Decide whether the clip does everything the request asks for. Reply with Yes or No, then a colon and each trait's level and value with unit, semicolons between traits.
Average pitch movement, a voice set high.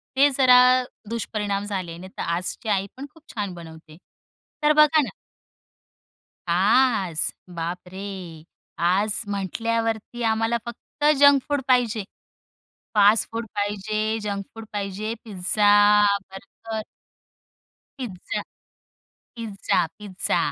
Yes: average, 3.2 semitones; high, 210 Hz